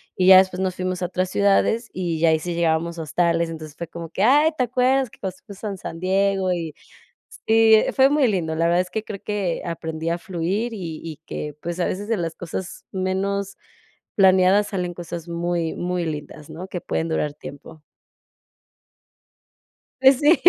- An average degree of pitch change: Yes, average, 3.1 semitones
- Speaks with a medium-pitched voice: Yes, medium, 180 Hz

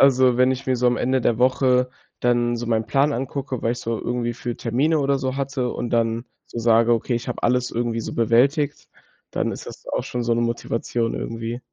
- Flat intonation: Yes, narrow, 1.9 semitones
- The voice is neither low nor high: No, low, 120 Hz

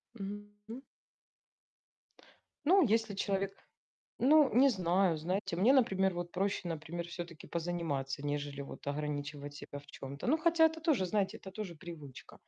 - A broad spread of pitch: Yes, wide, 6.1 semitones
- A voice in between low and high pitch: Yes, medium, 180 Hz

